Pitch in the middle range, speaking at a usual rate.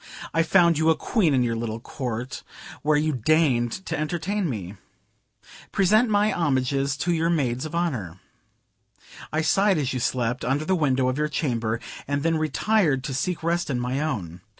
Yes: medium, 150 Hz; average, 175 wpm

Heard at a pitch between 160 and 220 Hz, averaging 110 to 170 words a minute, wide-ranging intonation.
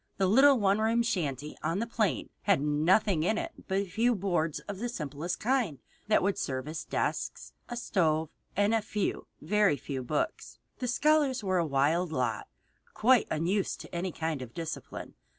No: high, 190 Hz; average, 180 wpm; wide, 6.0 semitones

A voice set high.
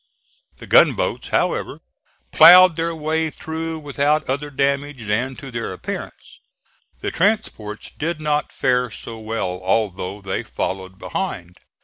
No: low, 135 Hz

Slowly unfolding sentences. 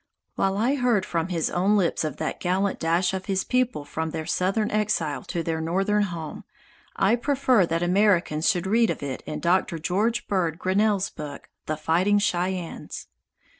No: average, 170 wpm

